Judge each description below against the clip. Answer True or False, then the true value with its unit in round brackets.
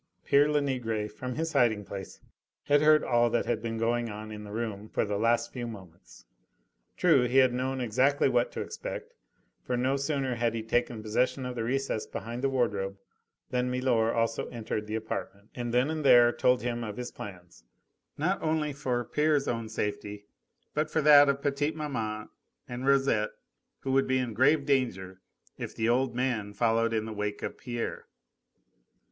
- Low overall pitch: True (120 Hz)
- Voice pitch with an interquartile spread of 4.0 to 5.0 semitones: False (3.6 semitones)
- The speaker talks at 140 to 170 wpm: False (180 wpm)